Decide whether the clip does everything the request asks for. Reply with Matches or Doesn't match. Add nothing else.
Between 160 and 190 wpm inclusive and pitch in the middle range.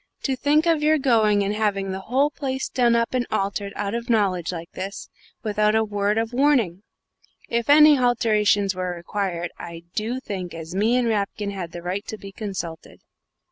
Doesn't match